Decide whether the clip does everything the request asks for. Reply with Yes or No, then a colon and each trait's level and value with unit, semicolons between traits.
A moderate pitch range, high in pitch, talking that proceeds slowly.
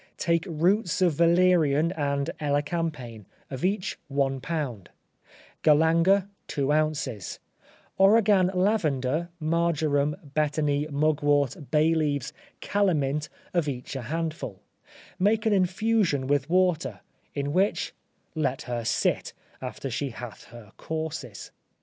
No: average, 3.6 semitones; medium, 155 Hz; slow, 110 wpm